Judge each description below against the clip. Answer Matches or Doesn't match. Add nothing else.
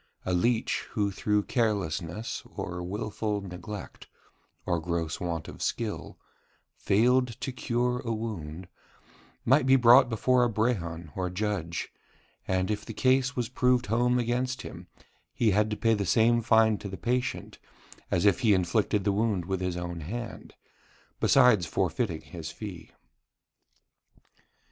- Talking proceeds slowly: Doesn't match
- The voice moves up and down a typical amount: Matches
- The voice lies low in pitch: Matches